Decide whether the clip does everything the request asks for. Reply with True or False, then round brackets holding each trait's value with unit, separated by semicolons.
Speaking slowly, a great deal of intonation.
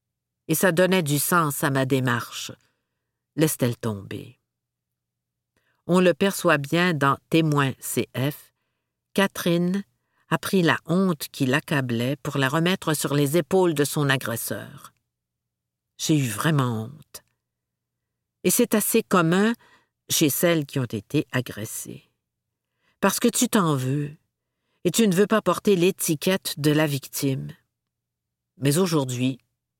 True (130 wpm; 5.7 semitones)